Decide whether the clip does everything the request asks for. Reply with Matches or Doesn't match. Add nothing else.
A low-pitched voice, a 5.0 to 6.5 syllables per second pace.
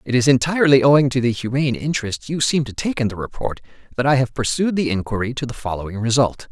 Doesn't match